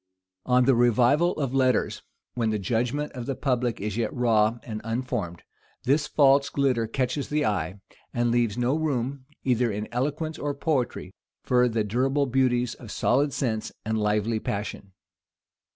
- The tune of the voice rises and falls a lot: No, average, 3.4 semitones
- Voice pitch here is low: Yes, low, 125 Hz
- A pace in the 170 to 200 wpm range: No, average, 155 wpm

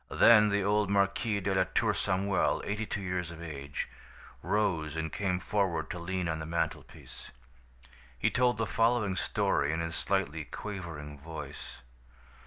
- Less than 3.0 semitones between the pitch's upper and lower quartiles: No, average, 4.1 semitones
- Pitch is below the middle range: Yes, very low, 95 Hz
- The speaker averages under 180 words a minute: Yes, average, 155 wpm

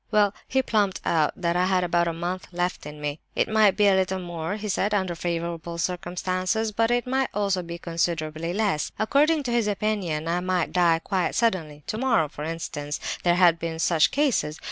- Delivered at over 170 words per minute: Yes, average, 185 wpm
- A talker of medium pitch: Yes, medium, 180 Hz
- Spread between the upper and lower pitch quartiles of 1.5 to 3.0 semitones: No, average, 3.9 semitones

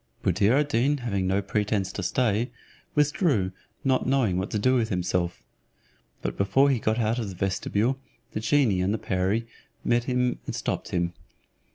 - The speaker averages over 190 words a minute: No, average, 170 wpm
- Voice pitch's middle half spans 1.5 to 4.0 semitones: No, average, 5.0 semitones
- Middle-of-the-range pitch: No, low, 110 Hz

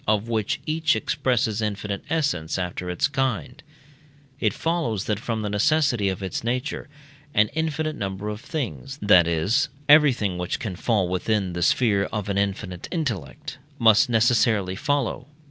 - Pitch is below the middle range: Yes, low, 110 Hz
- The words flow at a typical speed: Yes, average, 150 wpm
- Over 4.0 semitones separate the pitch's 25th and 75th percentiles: Yes, average, 5.3 semitones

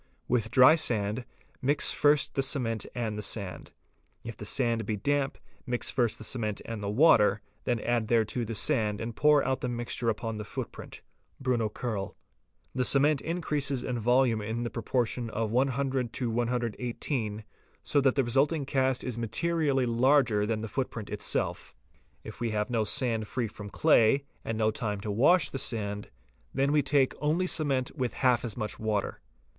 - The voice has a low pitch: Yes, low, 120 Hz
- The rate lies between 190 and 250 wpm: No, average, 175 wpm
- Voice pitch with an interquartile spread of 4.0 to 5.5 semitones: No, average, 3.5 semitones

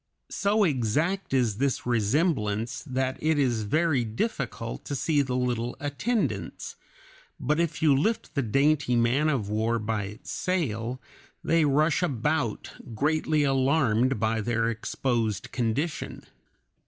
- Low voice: Yes, low, 130 Hz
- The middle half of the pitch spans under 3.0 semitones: No, average, 5.2 semitones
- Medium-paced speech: No, slow, 130 wpm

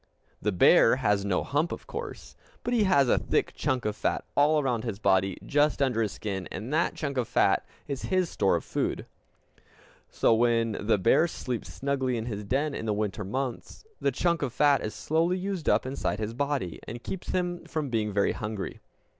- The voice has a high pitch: No, low, 125 Hz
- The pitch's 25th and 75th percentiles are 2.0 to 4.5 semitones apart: No, wide, 5.6 semitones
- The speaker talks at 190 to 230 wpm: Yes, average, 200 wpm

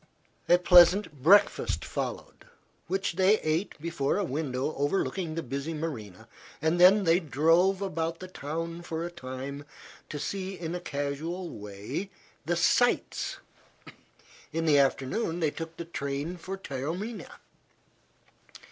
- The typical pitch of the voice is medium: Yes, medium, 165 Hz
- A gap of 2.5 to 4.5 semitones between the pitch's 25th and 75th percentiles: Yes, average, 4.1 semitones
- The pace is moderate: No, slow, 130 wpm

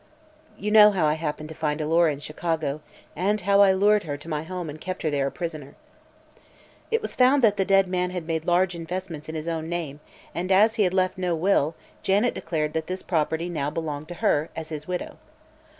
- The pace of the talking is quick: Yes, fast, 220 wpm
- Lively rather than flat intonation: No, average, 3.4 semitones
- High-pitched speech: No, medium, 170 Hz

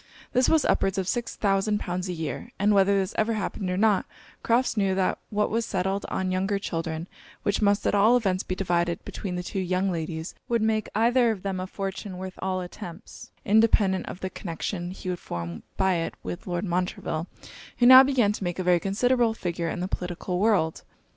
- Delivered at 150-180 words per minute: No, fast, 205 wpm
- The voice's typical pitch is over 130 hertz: Yes, high, 190 Hz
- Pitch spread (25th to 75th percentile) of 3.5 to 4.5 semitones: No, average, 2.9 semitones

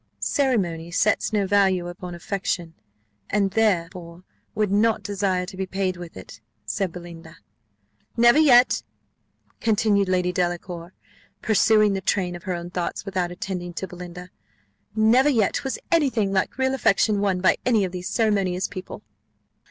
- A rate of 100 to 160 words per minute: Yes, average, 150 wpm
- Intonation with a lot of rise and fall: No, average, 3.1 semitones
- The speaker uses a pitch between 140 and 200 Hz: Yes, high, 190 Hz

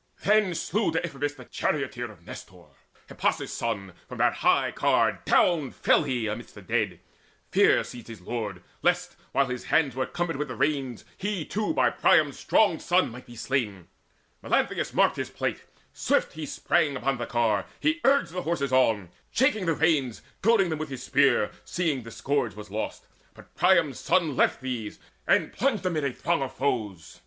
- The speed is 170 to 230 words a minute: Yes, average, 180 wpm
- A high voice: No, medium, 140 Hz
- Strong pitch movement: Yes, wide, 6.3 semitones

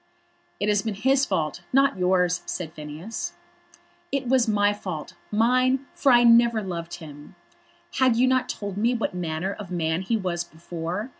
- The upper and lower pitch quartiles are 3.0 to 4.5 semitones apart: No, wide, 5.6 semitones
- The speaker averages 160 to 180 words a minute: Yes, average, 165 wpm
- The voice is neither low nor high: No, high, 205 Hz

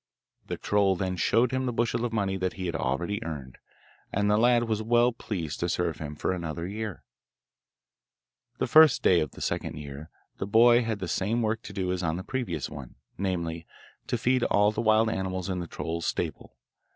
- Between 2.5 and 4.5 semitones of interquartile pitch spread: No, average, 4.9 semitones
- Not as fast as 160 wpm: No, average, 200 wpm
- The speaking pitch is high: No, very low, 95 Hz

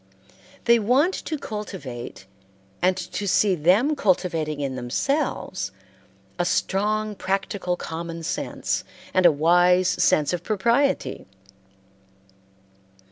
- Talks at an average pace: No, slow, 100 wpm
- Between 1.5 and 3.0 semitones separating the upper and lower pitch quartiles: No, average, 4.5 semitones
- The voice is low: No, medium, 185 Hz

